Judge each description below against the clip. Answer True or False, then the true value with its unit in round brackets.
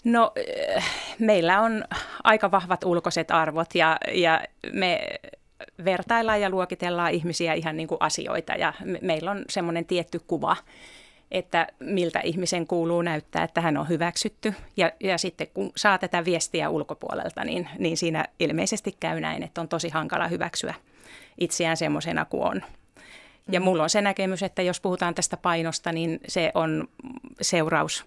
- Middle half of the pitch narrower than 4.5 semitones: True (2.9 semitones)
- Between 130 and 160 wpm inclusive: True (150 wpm)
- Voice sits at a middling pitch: True (175 Hz)